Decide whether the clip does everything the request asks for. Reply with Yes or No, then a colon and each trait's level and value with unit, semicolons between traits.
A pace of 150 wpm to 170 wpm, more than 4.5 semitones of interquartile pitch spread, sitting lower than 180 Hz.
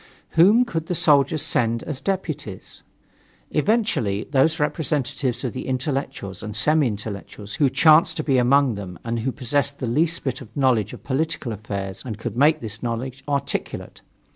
Yes: average, 165 wpm; average, 5.2 semitones; low, 135 Hz